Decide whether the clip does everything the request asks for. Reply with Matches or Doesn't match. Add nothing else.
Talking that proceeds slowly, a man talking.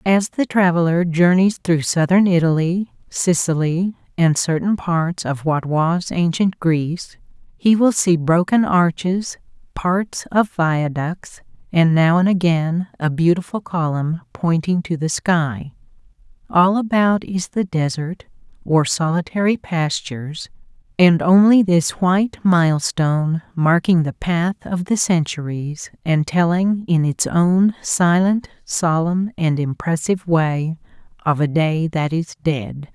Doesn't match